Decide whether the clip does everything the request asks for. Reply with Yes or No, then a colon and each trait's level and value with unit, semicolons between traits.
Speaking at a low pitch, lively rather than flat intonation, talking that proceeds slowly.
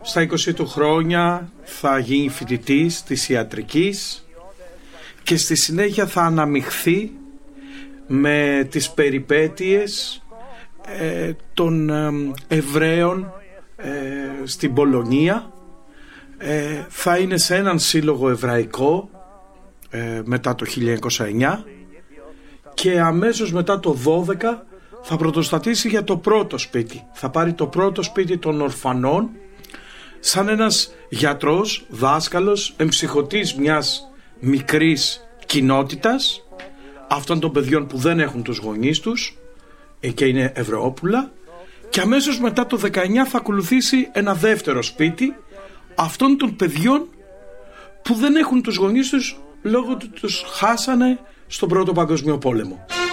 No: medium, 170 Hz; wide, 6.9 semitones; slow, 105 wpm